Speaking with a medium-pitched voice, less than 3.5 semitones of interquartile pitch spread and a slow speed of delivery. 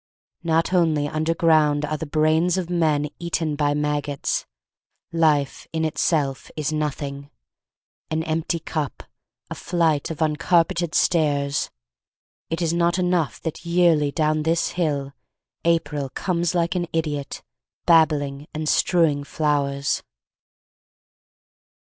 Yes: medium, 155 Hz; narrow, 2.4 semitones; slow, 120 wpm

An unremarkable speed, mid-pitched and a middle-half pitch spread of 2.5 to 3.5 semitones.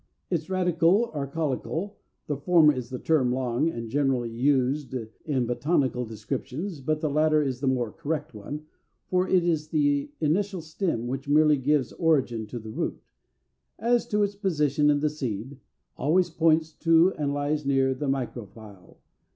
No: average, 165 wpm; medium, 145 Hz; average, 4.1 semitones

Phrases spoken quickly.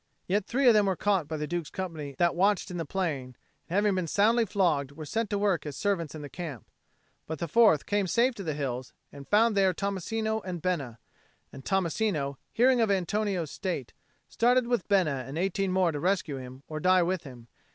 Yes: fast, 210 wpm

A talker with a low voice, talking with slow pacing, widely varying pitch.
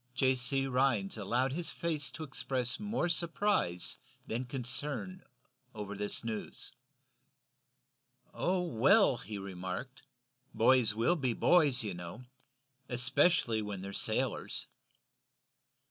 Yes: low, 125 Hz; slow, 110 wpm; wide, 6.1 semitones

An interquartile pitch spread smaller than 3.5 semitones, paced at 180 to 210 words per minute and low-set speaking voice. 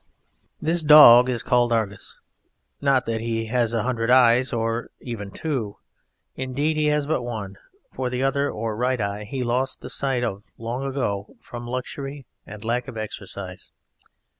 No: average, 2.8 semitones; average, 165 wpm; low, 120 Hz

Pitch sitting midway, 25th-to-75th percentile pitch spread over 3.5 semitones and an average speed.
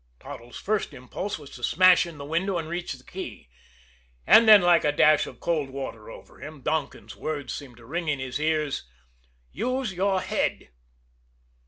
Yes: medium, 155 Hz; average, 4.6 semitones; average, 175 wpm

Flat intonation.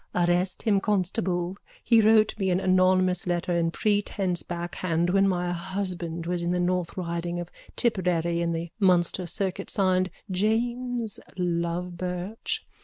Yes: narrow, 2.1 semitones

